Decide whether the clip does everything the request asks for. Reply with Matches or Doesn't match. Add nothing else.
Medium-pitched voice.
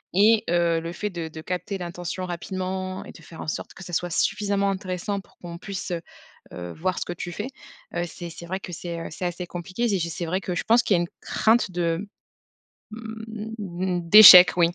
Matches